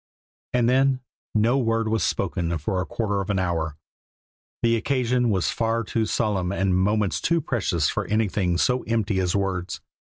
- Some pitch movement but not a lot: Yes, average, 3.8 semitones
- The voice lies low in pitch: Yes, low, 105 Hz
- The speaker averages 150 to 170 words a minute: Yes, average, 165 wpm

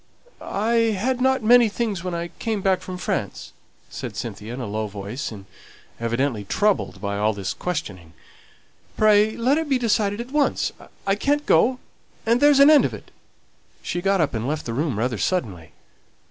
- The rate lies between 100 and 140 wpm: No, average, 175 wpm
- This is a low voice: No, medium, 185 Hz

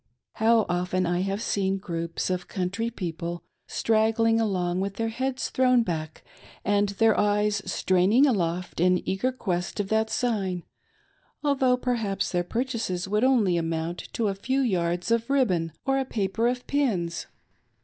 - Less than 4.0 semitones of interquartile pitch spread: No, average, 4.5 semitones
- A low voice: No, high, 200 Hz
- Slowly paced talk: No, average, 150 wpm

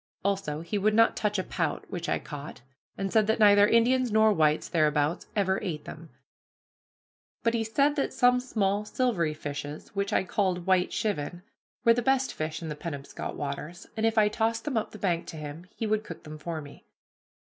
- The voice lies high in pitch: Yes, high, 195 Hz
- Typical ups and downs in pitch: No, wide, 5.8 semitones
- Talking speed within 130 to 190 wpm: No, fast, 205 wpm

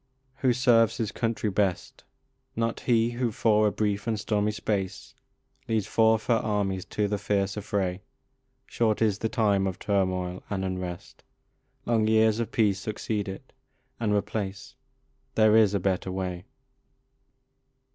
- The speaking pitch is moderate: No, low, 105 Hz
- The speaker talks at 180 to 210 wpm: No, average, 145 wpm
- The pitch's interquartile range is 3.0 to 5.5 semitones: No, narrow, 2.5 semitones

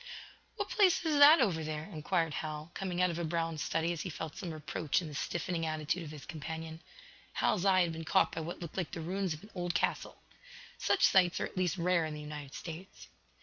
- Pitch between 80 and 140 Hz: No, medium, 165 Hz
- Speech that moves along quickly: Yes, fast, 230 wpm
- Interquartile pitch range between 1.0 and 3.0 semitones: Yes, average, 2.7 semitones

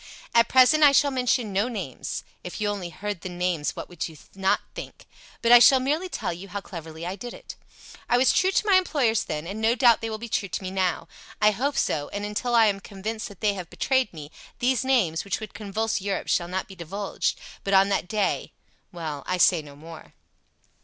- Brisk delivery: Yes, fast, 225 wpm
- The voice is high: Yes, high, 205 Hz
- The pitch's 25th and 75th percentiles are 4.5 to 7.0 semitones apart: Yes, average, 5.0 semitones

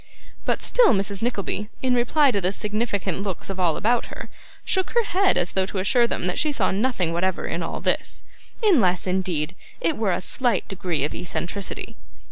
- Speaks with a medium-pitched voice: No, high, 195 Hz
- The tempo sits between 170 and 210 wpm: Yes, average, 190 wpm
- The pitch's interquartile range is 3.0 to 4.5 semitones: No, average, 4.9 semitones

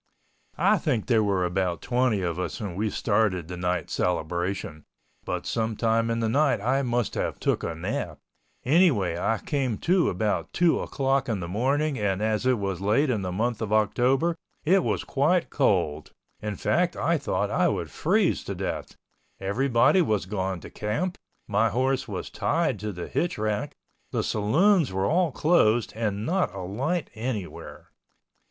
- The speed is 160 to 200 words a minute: Yes, average, 170 wpm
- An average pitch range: No, wide, 5.7 semitones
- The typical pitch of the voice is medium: No, low, 110 Hz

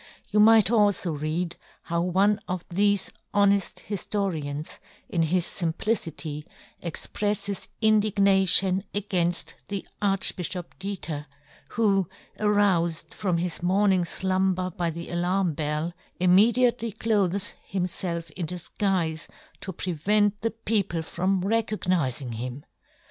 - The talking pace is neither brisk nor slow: No, slow, 105 wpm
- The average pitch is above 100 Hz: Yes, medium, 185 Hz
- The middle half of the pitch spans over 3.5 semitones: No, average, 3.2 semitones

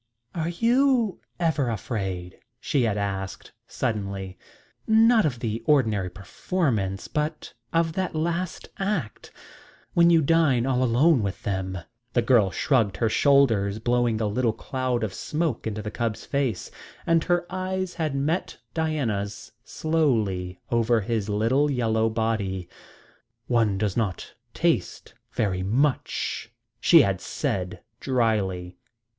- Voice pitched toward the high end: No, low, 120 Hz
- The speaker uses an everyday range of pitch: No, wide, 7.3 semitones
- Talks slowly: Yes, slow, 125 wpm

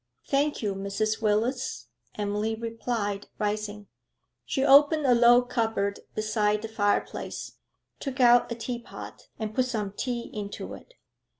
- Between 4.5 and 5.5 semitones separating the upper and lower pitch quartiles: No, average, 2.9 semitones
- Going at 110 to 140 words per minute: Yes, slow, 135 wpm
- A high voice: Yes, high, 225 Hz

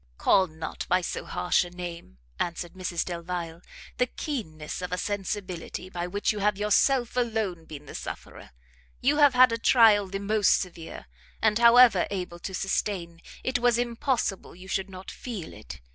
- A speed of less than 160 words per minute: No, average, 170 wpm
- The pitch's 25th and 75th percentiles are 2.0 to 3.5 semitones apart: No, average, 4.6 semitones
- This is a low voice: No, high, 190 Hz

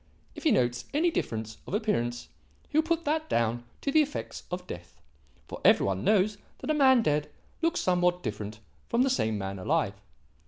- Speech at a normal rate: Yes, average, 190 wpm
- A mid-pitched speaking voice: Yes, medium, 180 Hz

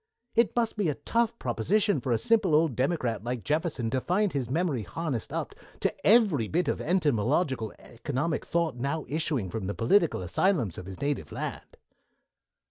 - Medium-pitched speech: Yes, medium, 145 Hz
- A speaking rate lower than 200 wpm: Yes, average, 170 wpm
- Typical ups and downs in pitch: No, wide, 6.9 semitones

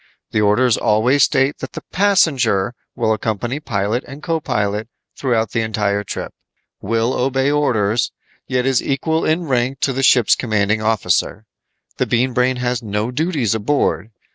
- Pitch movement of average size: Yes, average, 3.9 semitones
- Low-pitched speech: Yes, low, 120 Hz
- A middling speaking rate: Yes, average, 155 wpm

